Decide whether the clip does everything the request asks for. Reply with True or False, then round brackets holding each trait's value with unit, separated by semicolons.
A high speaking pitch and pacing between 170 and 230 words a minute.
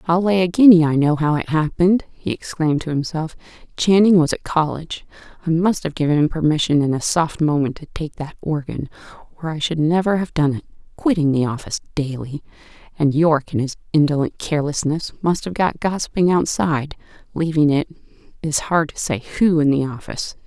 False (160 Hz; 180 wpm)